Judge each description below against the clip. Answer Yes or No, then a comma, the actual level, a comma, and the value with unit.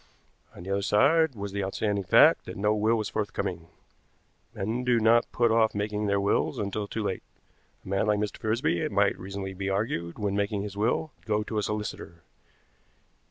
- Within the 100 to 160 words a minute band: No, average, 195 wpm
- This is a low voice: Yes, low, 105 Hz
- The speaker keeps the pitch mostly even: Yes, narrow, 2.0 semitones